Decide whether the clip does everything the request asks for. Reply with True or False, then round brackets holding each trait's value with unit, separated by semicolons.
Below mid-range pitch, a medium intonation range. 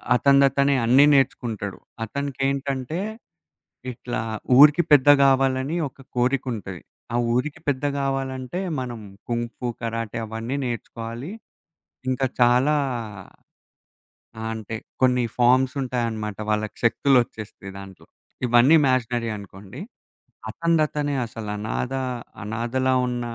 True (125 Hz; 3.1 semitones)